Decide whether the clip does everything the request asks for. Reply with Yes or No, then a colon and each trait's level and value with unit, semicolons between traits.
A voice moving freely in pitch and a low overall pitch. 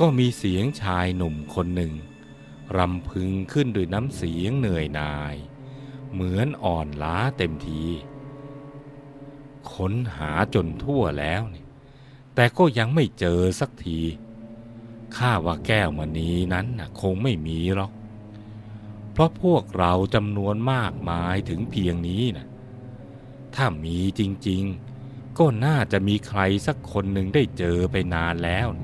Yes: wide, 6.3 semitones; low, 105 Hz